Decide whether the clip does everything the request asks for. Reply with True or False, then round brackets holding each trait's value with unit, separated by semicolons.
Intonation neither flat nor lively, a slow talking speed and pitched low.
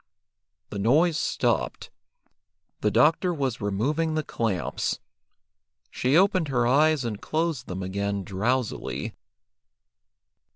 False (7.3 semitones; 100 wpm; 125 Hz)